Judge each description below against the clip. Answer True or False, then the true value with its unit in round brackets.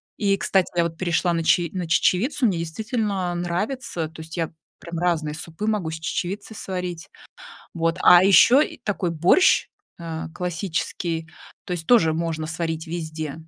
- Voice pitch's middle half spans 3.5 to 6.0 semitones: False (2.9 semitones)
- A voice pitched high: False (175 Hz)